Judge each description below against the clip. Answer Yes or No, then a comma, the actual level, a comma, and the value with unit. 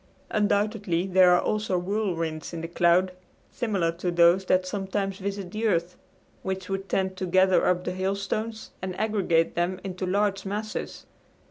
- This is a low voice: No, high, 190 Hz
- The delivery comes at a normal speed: Yes, average, 155 wpm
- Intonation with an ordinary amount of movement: No, narrow, 2.1 semitones